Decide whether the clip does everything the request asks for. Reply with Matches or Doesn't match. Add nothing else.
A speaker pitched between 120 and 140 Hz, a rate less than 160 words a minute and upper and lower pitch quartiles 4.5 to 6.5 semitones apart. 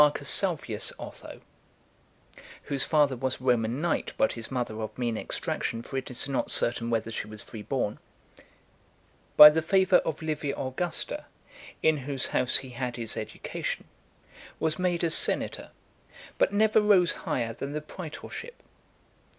Matches